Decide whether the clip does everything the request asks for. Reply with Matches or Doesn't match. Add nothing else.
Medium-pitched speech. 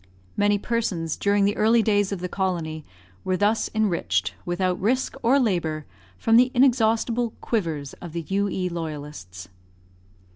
Doesn't match